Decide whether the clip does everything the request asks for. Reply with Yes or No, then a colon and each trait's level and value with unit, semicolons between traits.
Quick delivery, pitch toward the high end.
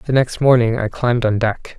No: fast, 235 wpm; low, 120 Hz